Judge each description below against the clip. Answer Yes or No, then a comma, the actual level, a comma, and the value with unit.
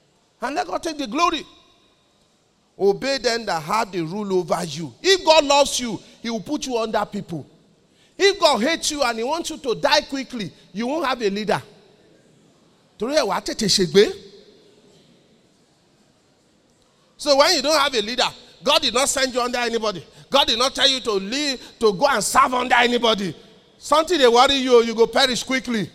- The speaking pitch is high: Yes, high, 245 Hz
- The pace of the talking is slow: No, average, 175 wpm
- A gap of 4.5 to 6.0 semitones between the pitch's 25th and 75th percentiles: Yes, wide, 5.4 semitones